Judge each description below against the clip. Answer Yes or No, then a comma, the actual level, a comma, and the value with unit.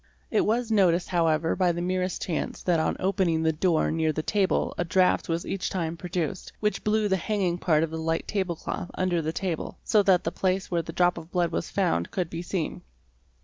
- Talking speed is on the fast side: Yes, fast, 220 wpm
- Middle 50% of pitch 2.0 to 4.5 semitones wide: Yes, narrow, 2.5 semitones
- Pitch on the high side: No, medium, 175 Hz